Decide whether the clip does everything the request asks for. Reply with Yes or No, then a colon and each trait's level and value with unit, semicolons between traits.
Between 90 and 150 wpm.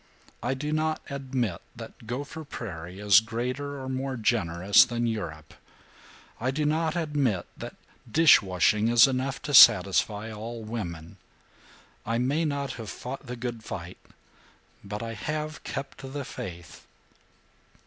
Yes: average, 140 wpm